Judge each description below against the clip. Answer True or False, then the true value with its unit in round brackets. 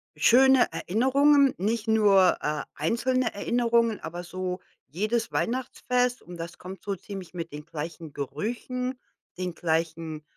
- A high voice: True (200 Hz)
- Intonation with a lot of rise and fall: True (6.5 semitones)